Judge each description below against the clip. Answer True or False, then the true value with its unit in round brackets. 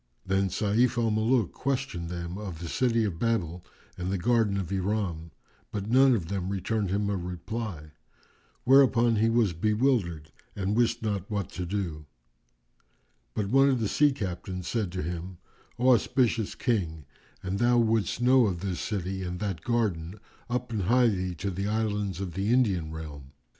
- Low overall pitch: True (100 Hz)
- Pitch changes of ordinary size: True (4.5 semitones)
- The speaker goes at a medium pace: True (170 wpm)